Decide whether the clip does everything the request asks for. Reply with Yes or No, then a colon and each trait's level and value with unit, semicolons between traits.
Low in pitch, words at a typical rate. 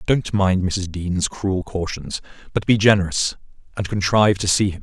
Yes: very low, 95 Hz; average, 175 wpm